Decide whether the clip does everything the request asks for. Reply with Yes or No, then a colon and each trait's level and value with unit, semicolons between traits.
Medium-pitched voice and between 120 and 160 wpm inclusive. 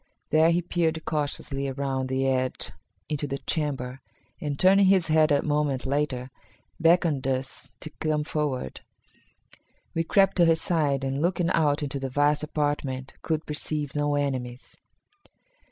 Yes: medium, 145 Hz; average, 145 wpm